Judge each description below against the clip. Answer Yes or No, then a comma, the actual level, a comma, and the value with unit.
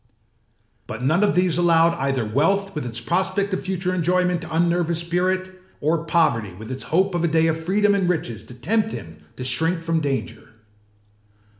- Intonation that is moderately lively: Yes, average, 4.7 semitones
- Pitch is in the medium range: Yes, medium, 170 Hz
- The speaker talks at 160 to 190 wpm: Yes, average, 185 wpm